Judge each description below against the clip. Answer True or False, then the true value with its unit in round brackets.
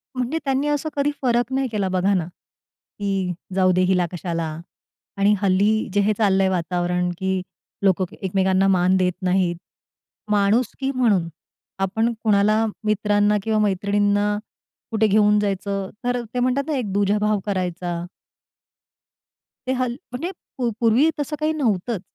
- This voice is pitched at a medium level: False (205 Hz)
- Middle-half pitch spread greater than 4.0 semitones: False (3.6 semitones)